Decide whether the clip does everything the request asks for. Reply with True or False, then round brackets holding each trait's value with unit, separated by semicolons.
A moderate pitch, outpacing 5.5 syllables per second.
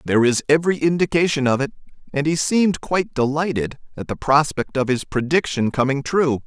True (145 Hz; 5.8 syllables/s)